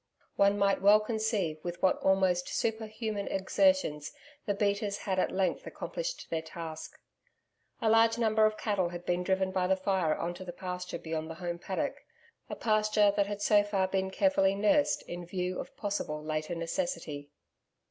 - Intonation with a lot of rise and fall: No, average, 3.3 semitones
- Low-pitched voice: No, high, 190 Hz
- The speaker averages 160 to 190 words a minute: Yes, average, 170 wpm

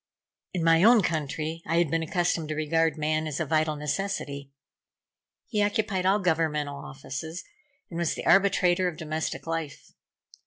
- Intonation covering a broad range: No, narrow, 2.6 semitones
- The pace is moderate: Yes, average, 155 wpm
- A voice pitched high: No, medium, 165 Hz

